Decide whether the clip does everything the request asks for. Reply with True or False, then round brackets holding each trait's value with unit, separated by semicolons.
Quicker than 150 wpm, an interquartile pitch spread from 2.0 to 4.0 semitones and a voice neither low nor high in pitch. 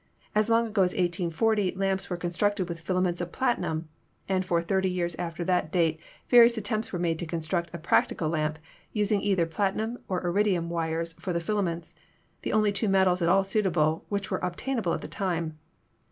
True (195 wpm; 3.2 semitones; 180 Hz)